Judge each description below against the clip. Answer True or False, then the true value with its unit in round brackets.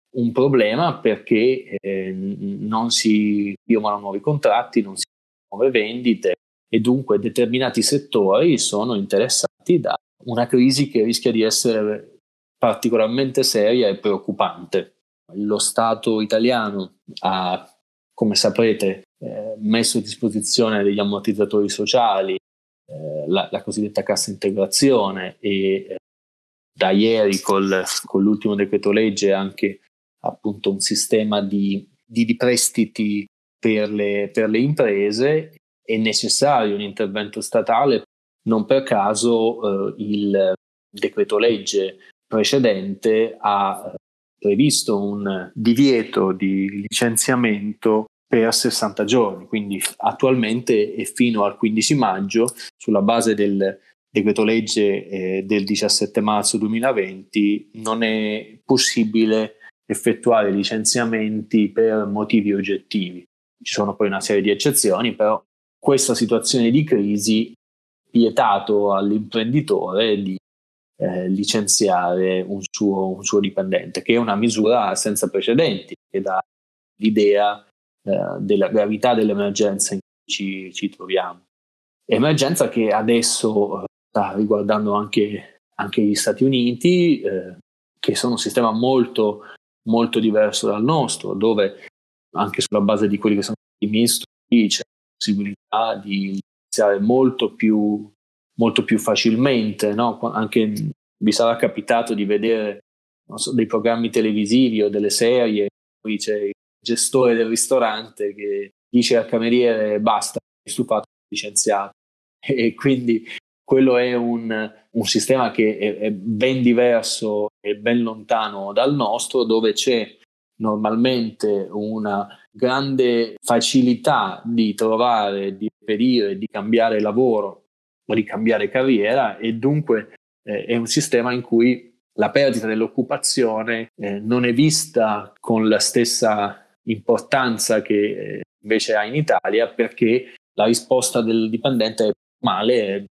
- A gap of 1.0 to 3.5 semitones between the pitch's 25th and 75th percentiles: True (2.5 semitones)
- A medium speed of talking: True (125 wpm)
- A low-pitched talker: True (110 Hz)